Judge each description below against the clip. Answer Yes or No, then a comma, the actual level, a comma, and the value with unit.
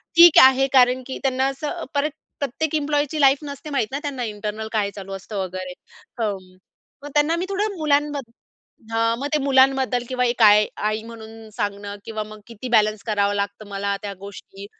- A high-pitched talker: Yes, high, 240 Hz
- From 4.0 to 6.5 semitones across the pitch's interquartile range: Yes, average, 5.2 semitones